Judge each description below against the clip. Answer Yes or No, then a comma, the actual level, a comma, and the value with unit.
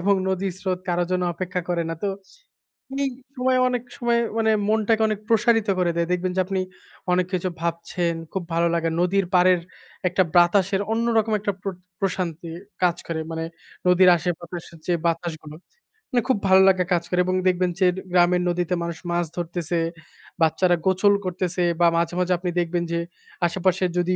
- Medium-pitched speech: Yes, medium, 180 Hz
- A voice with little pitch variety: Yes, narrow, 1.9 semitones